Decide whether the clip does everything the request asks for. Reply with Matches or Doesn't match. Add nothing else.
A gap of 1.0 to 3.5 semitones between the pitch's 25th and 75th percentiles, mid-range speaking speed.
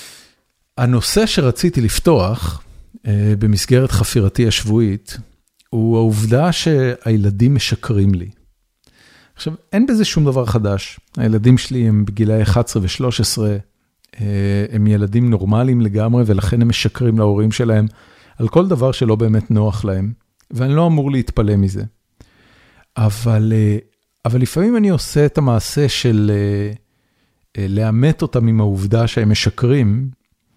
Matches